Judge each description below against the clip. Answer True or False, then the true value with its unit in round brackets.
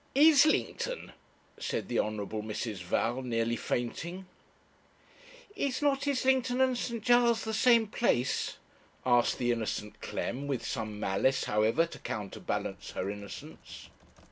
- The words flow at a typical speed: False (120 wpm)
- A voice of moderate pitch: False (130 Hz)